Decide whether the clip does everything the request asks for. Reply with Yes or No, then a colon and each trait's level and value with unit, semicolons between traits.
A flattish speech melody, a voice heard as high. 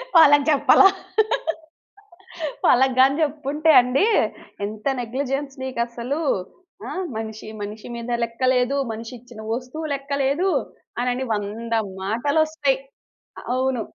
No: average, 3.3 semitones; very high, 255 Hz